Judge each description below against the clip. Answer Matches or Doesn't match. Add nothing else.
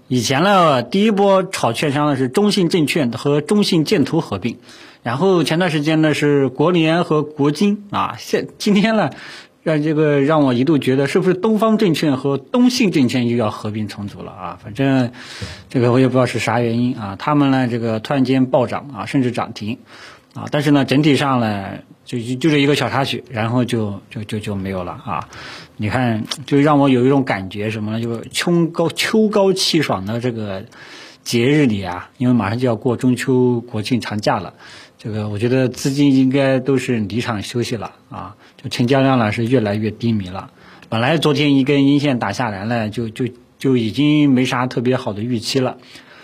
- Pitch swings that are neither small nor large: Matches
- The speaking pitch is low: Matches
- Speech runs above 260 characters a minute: Matches